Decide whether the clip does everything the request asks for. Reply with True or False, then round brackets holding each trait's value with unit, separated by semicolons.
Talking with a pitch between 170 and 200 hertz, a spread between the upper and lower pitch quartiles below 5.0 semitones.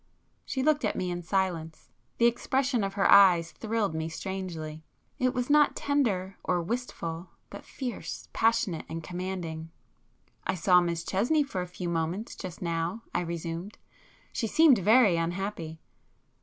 False (185 Hz; 5.3 semitones)